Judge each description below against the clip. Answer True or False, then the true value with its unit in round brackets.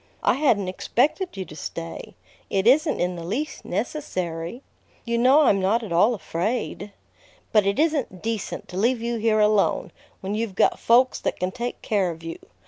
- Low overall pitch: False (215 Hz)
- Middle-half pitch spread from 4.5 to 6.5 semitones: True (5.0 semitones)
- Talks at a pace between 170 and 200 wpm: True (180 wpm)